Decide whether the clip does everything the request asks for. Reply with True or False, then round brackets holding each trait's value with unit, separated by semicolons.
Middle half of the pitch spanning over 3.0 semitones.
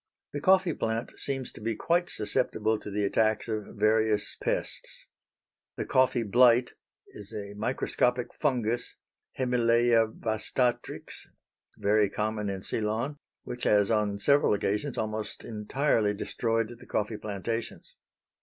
False (2.7 semitones)